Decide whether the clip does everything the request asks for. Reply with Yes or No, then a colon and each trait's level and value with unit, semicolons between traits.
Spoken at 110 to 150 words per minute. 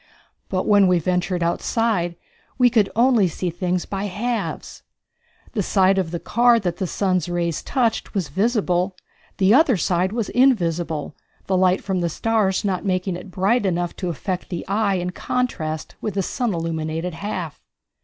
No: average, 165 wpm